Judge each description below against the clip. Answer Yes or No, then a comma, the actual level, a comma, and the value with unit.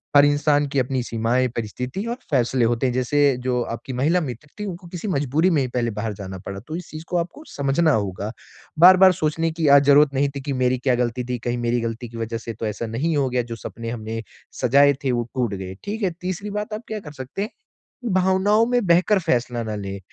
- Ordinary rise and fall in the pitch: No, wide, 5.9 semitones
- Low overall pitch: Yes, low, 130 Hz